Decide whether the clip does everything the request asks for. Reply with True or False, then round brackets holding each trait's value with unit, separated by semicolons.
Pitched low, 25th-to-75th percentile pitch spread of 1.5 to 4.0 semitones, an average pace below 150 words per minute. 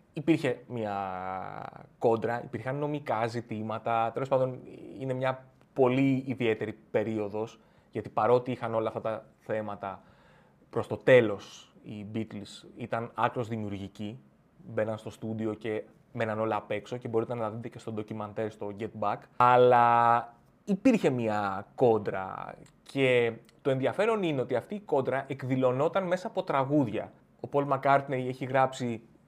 True (120 Hz; 3.2 semitones; 140 wpm)